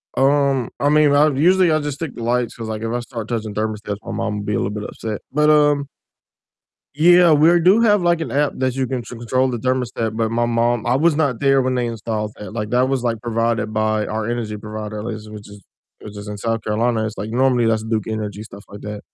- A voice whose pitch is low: Yes, low, 115 Hz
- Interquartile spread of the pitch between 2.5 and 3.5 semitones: No, average, 4.0 semitones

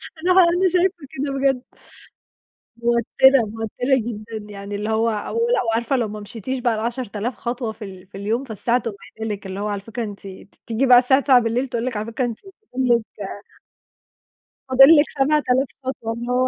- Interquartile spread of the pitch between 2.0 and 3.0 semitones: No, average, 3.5 semitones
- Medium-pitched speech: No, high, 235 Hz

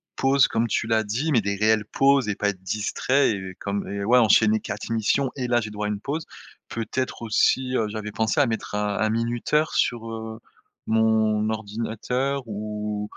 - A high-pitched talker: No, low, 110 Hz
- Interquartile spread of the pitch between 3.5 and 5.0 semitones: No, average, 2.7 semitones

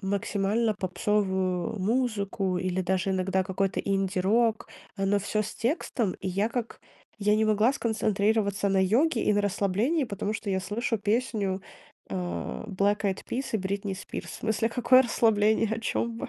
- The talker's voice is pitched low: No, high, 205 Hz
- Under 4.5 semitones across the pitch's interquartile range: Yes, average, 2.8 semitones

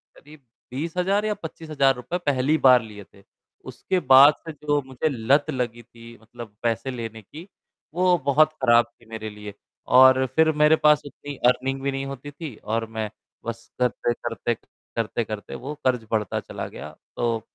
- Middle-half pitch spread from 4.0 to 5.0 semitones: Yes, average, 4.4 semitones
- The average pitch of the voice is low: Yes, low, 130 Hz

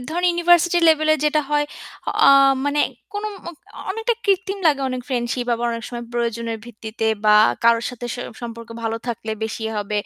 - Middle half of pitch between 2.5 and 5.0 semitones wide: No, wide, 5.6 semitones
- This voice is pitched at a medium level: No, high, 245 Hz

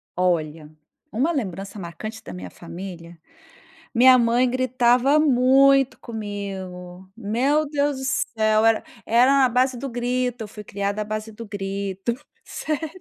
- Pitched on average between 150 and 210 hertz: No, high, 225 Hz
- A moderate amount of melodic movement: Yes, average, 4.7 semitones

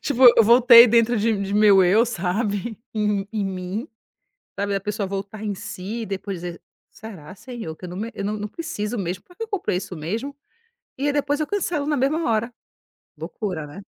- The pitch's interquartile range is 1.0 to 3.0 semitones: No, average, 3.7 semitones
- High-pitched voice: Yes, high, 210 Hz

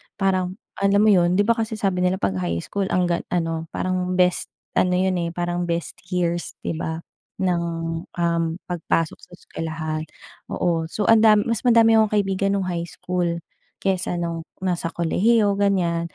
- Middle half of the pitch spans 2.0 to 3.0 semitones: Yes, average, 2.7 semitones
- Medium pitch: Yes, medium, 180 Hz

